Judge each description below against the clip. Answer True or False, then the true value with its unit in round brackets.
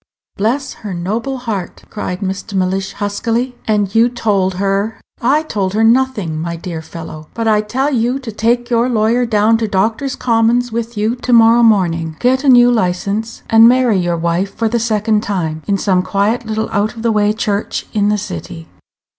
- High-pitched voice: True (215 Hz)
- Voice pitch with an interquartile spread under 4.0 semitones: True (3.2 semitones)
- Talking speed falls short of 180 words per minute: False (190 wpm)